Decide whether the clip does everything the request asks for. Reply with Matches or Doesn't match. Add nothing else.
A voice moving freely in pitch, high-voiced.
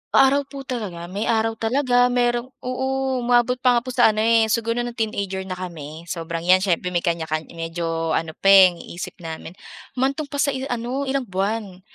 Matches